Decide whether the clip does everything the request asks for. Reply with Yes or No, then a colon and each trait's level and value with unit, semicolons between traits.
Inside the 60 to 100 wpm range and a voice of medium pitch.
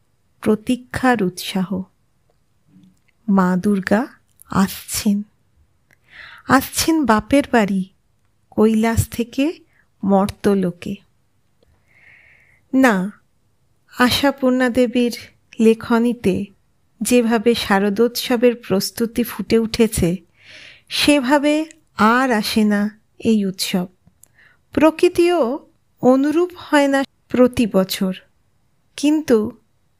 No: average, 65 wpm; high, 230 Hz